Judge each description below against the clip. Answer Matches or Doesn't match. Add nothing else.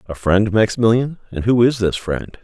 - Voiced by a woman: Doesn't match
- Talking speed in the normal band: Matches